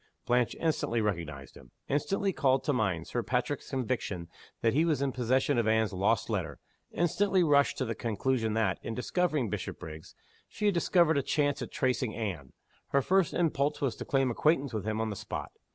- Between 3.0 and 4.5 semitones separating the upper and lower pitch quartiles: No, average, 5.2 semitones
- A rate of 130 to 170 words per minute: No, average, 185 wpm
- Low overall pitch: Yes, low, 125 Hz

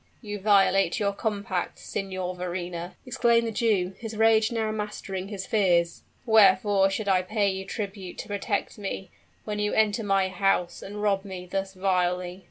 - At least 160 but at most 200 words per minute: Yes, average, 165 wpm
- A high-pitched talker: Yes, high, 195 Hz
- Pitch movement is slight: Yes, narrow, 2.2 semitones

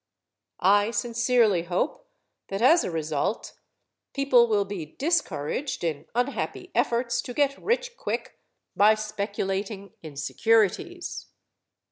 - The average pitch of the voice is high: Yes, high, 220 Hz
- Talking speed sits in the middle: No, slow, 110 wpm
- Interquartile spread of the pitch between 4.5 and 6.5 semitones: Yes, average, 5.2 semitones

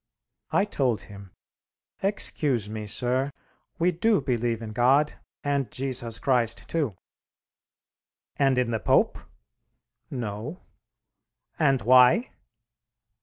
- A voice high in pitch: No, low, 125 Hz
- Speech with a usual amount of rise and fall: Yes, average, 3.7 semitones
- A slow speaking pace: Yes, slow, 100 wpm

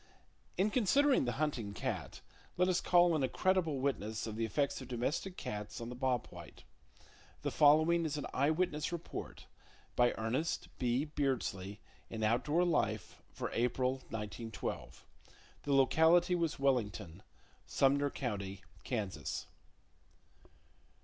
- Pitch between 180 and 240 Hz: No, low, 135 Hz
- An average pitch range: No, wide, 6.0 semitones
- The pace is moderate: No, slow, 130 wpm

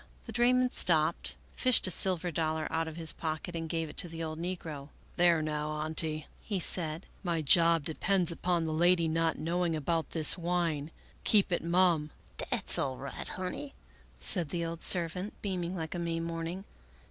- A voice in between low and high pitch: Yes, medium, 165 Hz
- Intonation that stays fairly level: Yes, narrow, 2.1 semitones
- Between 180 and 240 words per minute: Yes, average, 185 wpm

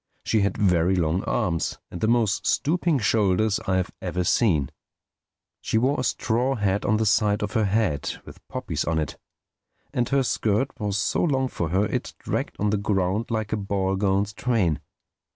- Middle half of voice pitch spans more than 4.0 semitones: No, average, 3.2 semitones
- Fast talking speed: No, average, 185 wpm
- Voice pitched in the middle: No, low, 105 Hz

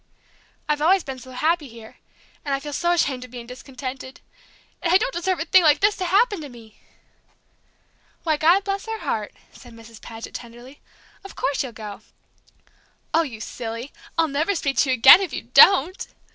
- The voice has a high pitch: Yes, very high, 285 Hz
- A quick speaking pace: No, average, 185 wpm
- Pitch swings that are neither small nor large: No, wide, 6.1 semitones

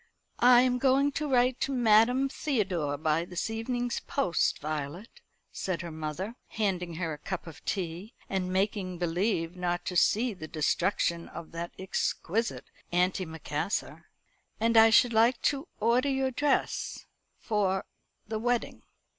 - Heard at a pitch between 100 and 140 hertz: No, high, 195 Hz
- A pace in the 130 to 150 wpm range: Yes, average, 140 wpm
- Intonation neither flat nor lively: No, wide, 6.0 semitones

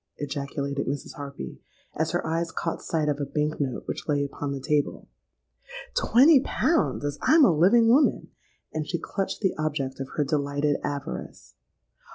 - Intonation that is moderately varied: Yes, average, 3.1 semitones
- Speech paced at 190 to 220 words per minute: No, average, 165 wpm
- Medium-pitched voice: Yes, medium, 150 Hz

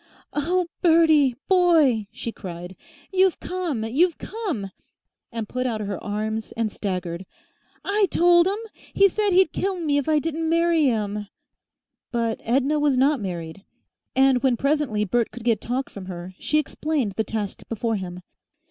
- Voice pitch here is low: No, very high, 255 Hz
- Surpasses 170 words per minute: No, average, 155 wpm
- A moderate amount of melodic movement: No, wide, 7.5 semitones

